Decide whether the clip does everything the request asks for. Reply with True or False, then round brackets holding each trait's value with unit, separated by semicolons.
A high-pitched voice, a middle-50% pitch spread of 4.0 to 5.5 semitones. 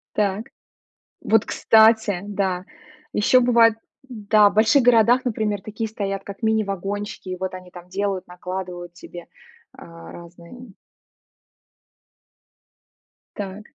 False (205 Hz; 3.1 semitones)